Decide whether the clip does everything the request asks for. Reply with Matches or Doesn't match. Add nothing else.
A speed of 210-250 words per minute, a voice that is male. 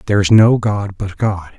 Matches